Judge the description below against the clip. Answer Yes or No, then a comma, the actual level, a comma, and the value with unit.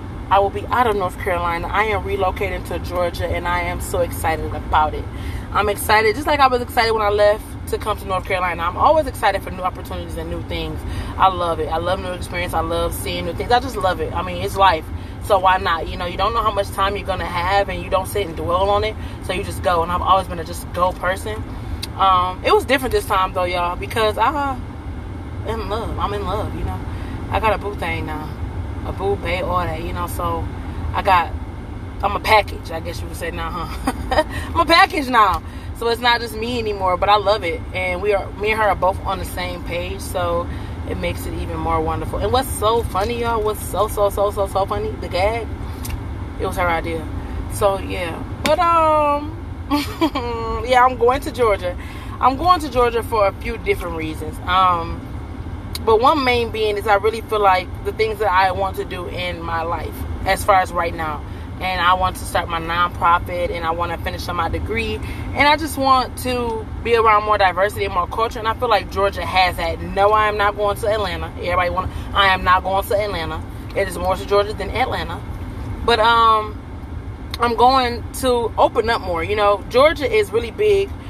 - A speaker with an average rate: No, fast, 225 wpm